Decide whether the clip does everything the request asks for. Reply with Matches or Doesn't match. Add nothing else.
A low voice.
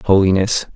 Matches